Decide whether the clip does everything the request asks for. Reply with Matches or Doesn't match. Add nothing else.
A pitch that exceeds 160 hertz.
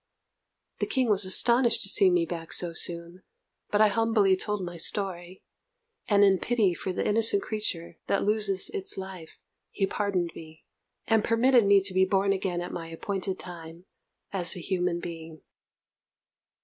Matches